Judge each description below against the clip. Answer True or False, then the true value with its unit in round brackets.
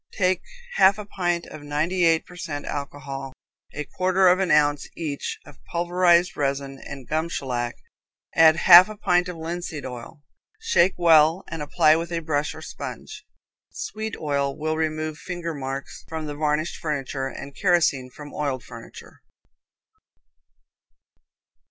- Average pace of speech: True (145 wpm)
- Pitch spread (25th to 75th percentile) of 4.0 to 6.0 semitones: False (3.4 semitones)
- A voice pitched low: False (155 Hz)